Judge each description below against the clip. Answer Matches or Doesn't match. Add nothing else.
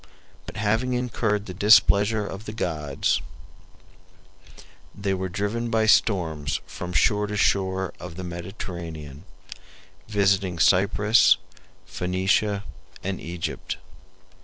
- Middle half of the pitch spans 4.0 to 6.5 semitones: Doesn't match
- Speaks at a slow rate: Matches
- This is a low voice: Matches